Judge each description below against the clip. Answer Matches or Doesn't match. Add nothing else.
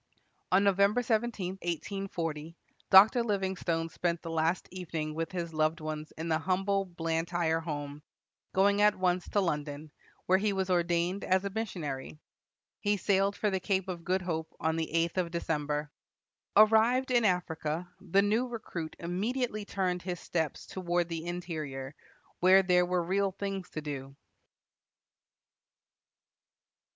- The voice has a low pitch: Doesn't match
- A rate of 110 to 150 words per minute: Matches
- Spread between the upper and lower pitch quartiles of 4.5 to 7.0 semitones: Doesn't match